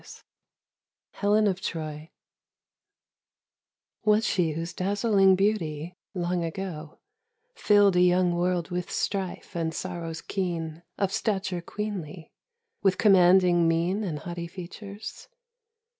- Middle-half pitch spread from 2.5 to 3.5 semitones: Yes, average, 2.8 semitones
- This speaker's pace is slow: Yes, slow, 110 wpm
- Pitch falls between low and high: Yes, medium, 180 Hz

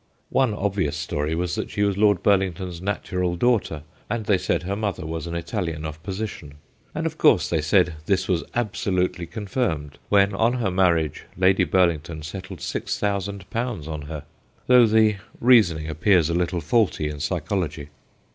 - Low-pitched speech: Yes, very low, 95 Hz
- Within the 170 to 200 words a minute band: No, average, 160 wpm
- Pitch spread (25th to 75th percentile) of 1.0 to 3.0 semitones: No, average, 4.1 semitones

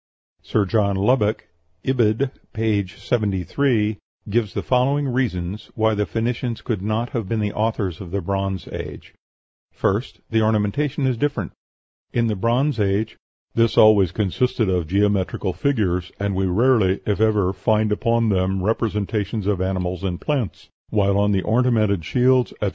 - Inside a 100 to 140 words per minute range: No, average, 150 wpm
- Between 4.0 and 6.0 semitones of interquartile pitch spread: No, average, 3.2 semitones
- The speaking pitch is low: Yes, low, 105 Hz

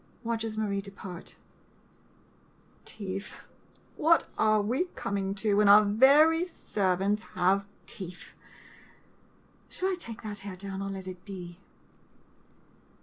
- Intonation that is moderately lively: No, narrow, 2.2 semitones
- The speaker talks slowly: Yes, slow, 115 wpm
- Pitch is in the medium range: No, high, 200 Hz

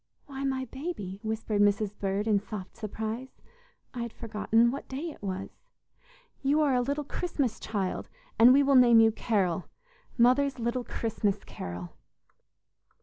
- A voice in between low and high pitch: No, high, 230 Hz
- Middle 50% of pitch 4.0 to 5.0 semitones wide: Yes, average, 4.3 semitones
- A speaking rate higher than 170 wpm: No, average, 145 wpm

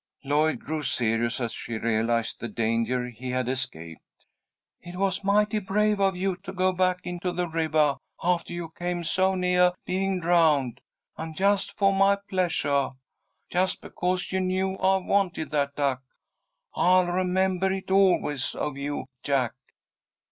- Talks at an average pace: Yes, average, 150 wpm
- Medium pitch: Yes, medium, 175 Hz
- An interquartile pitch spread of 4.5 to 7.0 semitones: Yes, average, 5.3 semitones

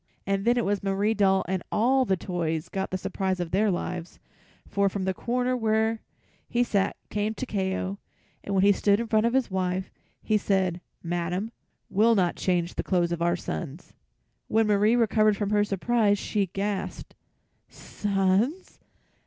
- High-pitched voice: Yes, high, 200 Hz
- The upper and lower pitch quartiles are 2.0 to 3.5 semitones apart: Yes, average, 2.7 semitones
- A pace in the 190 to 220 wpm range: No, average, 170 wpm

